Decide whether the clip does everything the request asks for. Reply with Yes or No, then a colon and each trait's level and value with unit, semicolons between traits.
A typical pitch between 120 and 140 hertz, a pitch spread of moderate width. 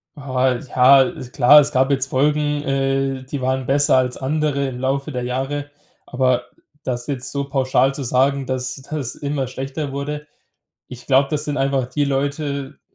No: low, 135 Hz; narrow, 1.6 semitones